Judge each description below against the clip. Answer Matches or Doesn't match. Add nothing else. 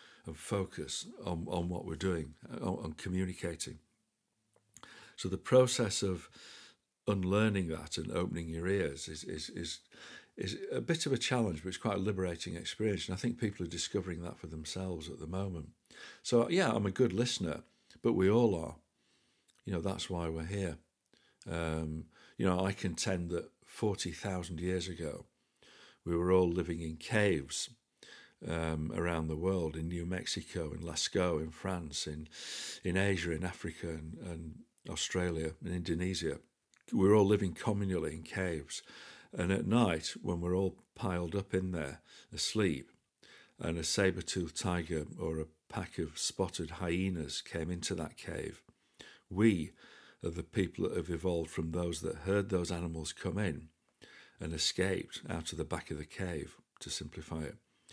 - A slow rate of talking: Doesn't match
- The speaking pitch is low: Matches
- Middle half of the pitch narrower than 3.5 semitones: Matches